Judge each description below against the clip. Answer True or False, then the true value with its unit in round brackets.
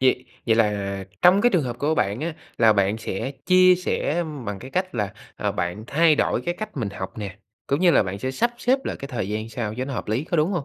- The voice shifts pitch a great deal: True (8.4 semitones)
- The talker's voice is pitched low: True (125 Hz)